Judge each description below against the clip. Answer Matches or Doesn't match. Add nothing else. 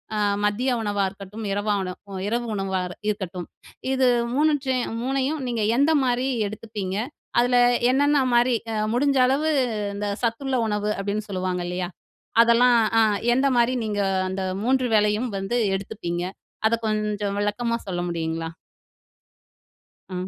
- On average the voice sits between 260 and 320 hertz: Doesn't match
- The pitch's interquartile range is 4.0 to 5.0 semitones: Matches